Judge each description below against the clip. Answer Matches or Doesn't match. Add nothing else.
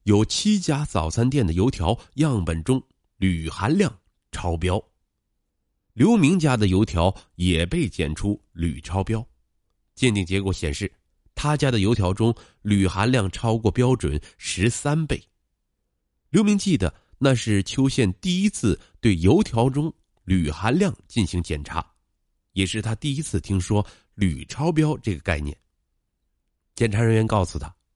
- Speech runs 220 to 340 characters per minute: Doesn't match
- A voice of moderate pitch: Doesn't match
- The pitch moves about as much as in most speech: Doesn't match